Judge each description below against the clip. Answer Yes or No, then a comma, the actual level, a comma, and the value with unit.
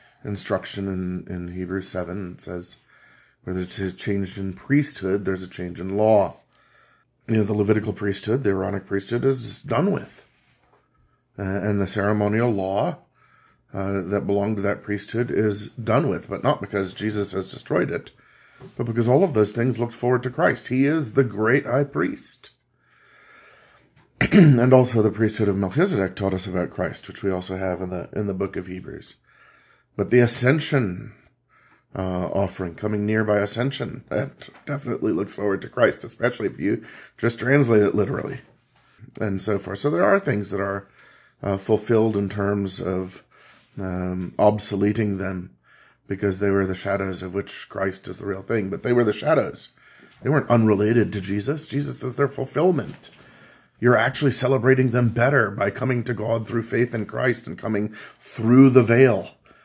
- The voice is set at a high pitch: No, low, 105 Hz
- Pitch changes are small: No, average, 4.1 semitones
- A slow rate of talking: No, average, 170 wpm